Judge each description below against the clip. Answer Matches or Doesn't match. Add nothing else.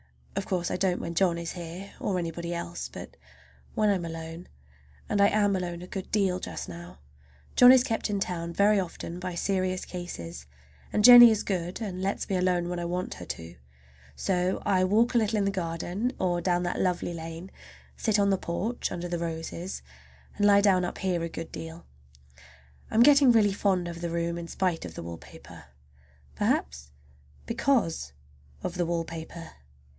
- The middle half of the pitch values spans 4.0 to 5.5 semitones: Doesn't match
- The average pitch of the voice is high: Doesn't match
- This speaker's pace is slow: Doesn't match